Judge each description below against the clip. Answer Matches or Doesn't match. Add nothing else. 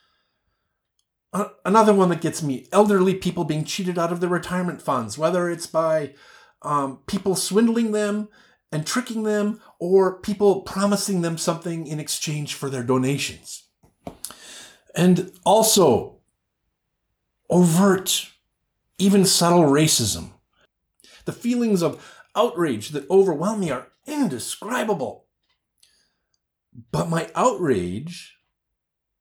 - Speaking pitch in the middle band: Matches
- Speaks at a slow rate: Matches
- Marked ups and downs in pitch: Doesn't match